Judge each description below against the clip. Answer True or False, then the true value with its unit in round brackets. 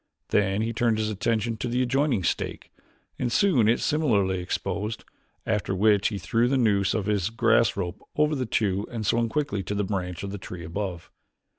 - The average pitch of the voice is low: True (110 Hz)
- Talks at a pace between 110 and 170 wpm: False (195 wpm)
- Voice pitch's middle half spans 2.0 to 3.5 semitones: True (3.2 semitones)